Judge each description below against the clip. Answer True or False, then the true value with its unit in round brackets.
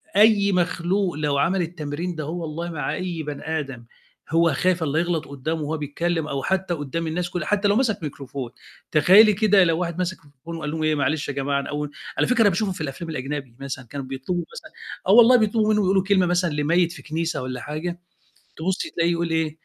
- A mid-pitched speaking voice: True (165 Hz)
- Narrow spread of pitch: False (3.7 semitones)